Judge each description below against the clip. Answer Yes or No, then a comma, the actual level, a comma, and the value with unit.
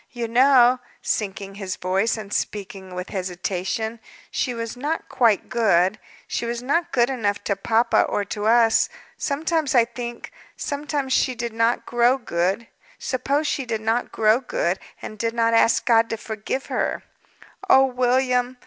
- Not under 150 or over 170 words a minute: No, average, 140 wpm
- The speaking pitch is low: No, high, 235 Hz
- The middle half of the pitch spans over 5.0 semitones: No, average, 3.2 semitones